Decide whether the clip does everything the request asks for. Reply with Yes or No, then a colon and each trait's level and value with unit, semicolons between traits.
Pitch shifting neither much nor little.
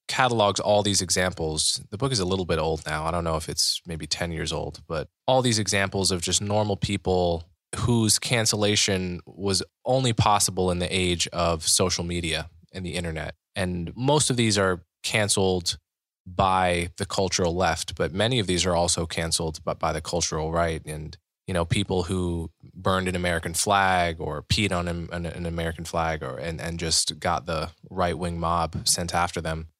Yes: average, 3.0 semitones